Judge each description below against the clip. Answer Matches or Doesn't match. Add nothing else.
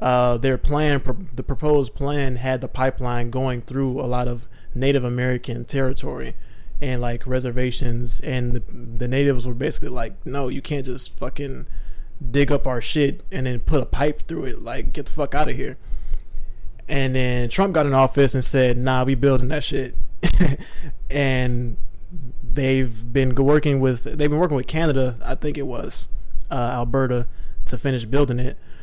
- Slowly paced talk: Doesn't match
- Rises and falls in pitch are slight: Matches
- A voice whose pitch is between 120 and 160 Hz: Matches